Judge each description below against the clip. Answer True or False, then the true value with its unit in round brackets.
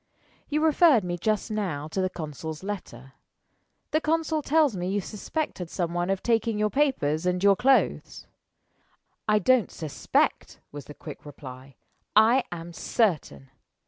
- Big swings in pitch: True (7.0 semitones)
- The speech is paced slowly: False (145 wpm)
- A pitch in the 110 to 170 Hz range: False (195 Hz)